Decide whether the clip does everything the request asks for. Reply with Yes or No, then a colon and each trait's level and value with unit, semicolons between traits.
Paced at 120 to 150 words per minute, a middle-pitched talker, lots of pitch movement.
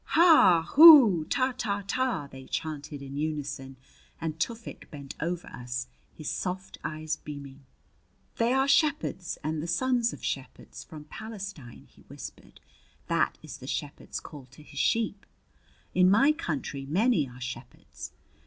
Yes: average, 145 wpm; medium, 165 Hz; wide, 8.2 semitones